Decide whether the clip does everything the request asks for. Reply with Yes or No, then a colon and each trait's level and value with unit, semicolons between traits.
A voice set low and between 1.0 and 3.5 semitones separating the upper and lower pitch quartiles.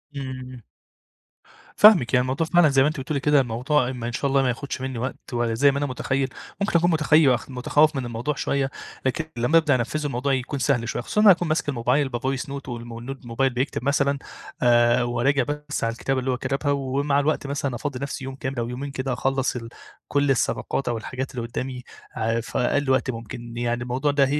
Yes: low, 130 Hz; narrow, 2.6 semitones